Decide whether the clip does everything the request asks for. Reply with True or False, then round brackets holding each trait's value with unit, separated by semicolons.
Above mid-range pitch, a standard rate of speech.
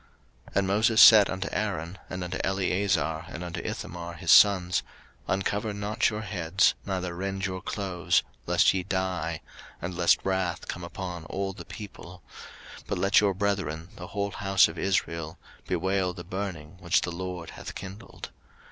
False (95 Hz; 160 wpm)